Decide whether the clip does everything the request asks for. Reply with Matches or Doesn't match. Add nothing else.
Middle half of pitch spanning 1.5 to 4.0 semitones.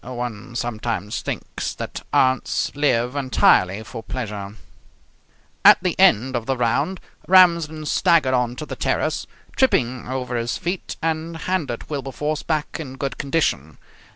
Doesn't match